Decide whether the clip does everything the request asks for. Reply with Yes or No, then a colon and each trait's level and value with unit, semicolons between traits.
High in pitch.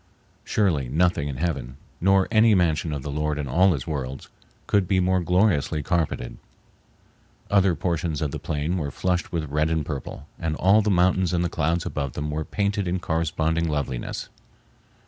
No: very low, 80 Hz